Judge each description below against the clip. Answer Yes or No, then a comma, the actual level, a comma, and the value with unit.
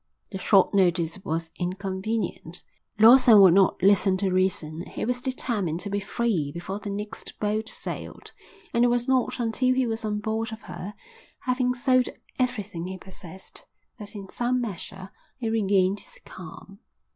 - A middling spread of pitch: Yes, average, 3.8 semitones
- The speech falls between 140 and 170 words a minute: Yes, average, 160 wpm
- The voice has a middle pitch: No, high, 205 Hz